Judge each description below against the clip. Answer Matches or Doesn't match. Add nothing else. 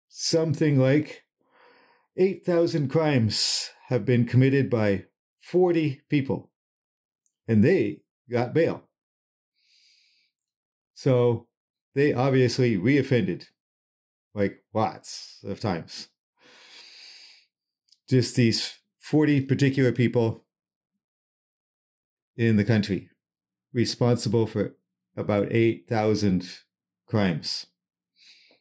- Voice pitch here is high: Doesn't match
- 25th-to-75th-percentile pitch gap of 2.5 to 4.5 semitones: Doesn't match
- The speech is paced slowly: Matches